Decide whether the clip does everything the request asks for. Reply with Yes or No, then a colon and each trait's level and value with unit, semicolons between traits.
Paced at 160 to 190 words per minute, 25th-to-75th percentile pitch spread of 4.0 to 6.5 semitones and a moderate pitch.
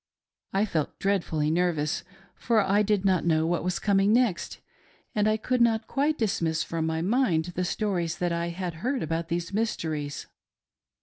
Yes: average, 170 wpm; average, 4.4 semitones; medium, 180 Hz